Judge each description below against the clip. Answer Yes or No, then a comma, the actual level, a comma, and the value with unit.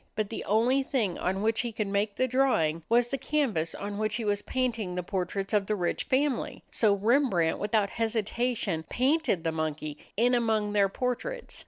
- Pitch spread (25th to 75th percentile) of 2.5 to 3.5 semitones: No, average, 4.0 semitones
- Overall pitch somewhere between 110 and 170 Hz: No, high, 215 Hz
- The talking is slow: No, average, 185 wpm